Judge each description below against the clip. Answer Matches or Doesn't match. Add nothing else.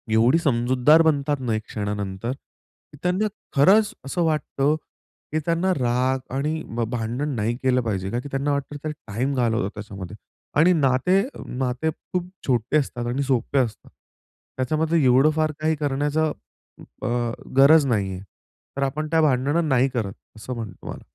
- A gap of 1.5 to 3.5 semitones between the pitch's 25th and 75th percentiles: Doesn't match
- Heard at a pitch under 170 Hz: Matches